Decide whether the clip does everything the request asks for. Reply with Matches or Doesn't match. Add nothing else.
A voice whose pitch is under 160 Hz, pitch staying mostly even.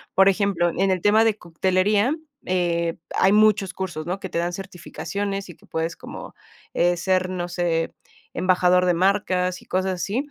Doesn't match